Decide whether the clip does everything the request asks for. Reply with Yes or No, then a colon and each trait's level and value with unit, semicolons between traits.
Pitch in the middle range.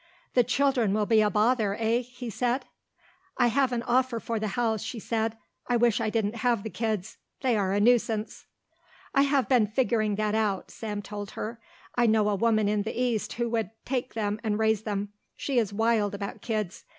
No: high, 225 Hz